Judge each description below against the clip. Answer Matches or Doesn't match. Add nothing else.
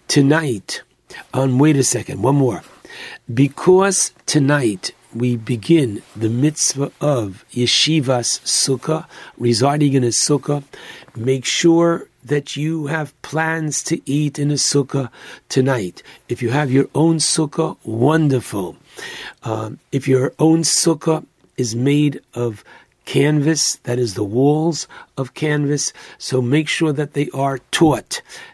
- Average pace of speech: Doesn't match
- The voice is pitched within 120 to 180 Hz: Matches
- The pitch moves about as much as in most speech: Matches